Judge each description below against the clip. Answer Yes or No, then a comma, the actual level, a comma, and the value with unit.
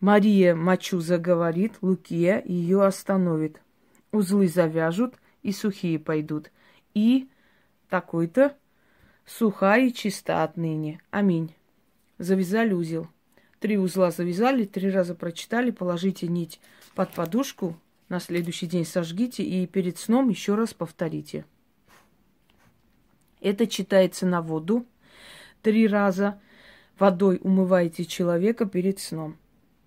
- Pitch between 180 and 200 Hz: Yes, high, 190 Hz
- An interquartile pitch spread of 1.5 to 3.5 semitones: Yes, average, 3.1 semitones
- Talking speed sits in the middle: No, slow, 100 wpm